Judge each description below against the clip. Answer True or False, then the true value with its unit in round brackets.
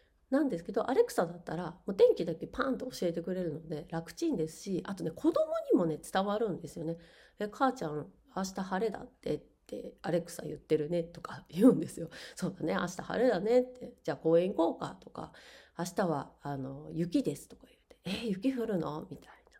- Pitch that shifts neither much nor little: False (6.8 semitones)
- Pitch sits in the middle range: True (180 Hz)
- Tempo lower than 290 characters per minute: False (390 characters per minute)